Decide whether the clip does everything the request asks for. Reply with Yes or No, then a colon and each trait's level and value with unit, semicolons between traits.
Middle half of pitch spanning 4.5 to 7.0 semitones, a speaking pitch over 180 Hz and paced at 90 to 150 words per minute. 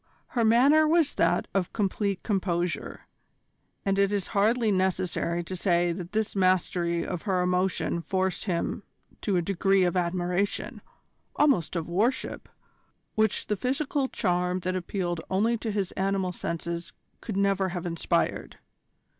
No: average, 2.8 semitones; high, 190 Hz; average, 140 wpm